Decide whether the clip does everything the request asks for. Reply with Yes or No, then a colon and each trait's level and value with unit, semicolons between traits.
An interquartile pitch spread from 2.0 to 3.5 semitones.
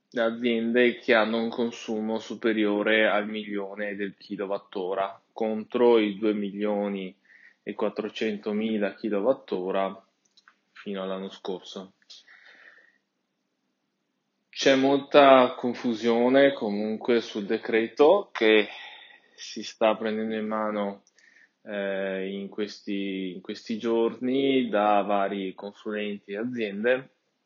Yes: narrow, 2.4 semitones